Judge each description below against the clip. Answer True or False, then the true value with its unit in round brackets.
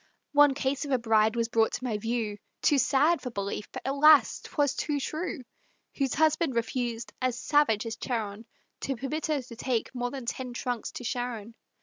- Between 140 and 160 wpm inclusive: False (190 wpm)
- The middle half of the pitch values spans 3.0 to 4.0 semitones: True (3.6 semitones)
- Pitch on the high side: True (250 Hz)